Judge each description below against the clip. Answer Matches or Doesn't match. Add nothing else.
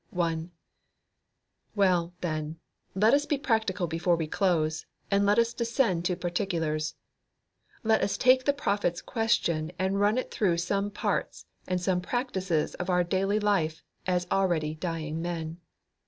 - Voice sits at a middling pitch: Matches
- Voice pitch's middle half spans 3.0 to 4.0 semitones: Matches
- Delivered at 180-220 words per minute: Doesn't match